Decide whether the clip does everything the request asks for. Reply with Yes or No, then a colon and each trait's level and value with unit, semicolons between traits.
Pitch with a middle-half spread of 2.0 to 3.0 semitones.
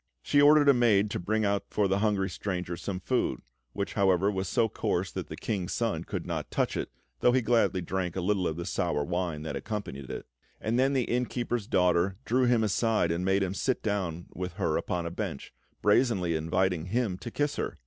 No: average, 4.2 semitones